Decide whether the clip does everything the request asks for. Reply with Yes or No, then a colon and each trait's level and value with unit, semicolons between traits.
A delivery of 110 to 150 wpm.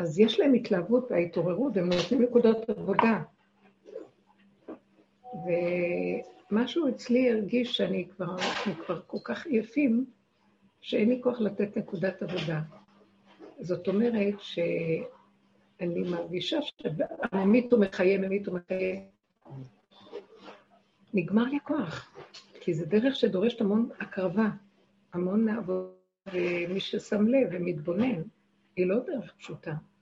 No: slow, 100 wpm